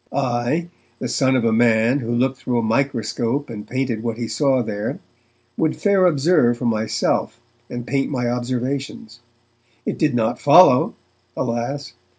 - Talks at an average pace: Yes, average, 155 wpm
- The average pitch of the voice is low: Yes, low, 120 Hz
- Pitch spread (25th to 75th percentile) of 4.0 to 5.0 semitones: No, average, 2.9 semitones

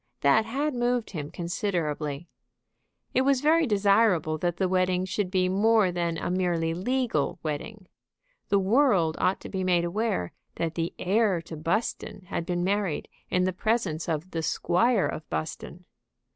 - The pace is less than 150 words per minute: No, average, 160 wpm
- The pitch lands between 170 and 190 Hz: Yes, medium, 185 Hz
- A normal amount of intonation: Yes, average, 4.6 semitones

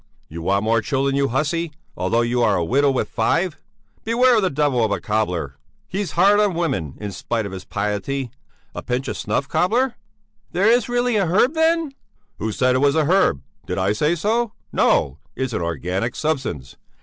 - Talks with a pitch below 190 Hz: Yes, low, 135 Hz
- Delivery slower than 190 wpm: No, average, 195 wpm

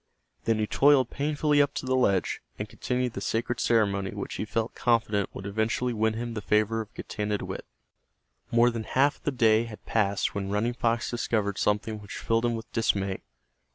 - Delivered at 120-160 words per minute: No, average, 190 wpm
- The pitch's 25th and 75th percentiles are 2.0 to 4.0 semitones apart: Yes, narrow, 2.5 semitones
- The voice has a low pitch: Yes, low, 115 Hz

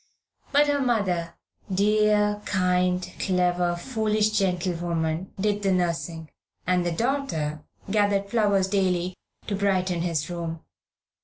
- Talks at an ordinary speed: No, slow, 110 wpm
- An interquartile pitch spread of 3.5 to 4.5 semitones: No, average, 3.1 semitones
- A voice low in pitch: No, medium, 185 Hz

